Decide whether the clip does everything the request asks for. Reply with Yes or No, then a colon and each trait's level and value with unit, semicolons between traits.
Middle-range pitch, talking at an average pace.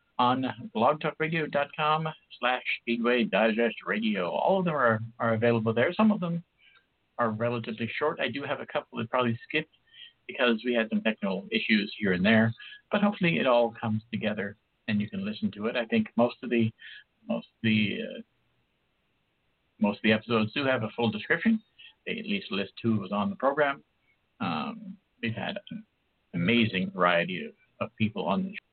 No: low, 125 Hz; average, 185 wpm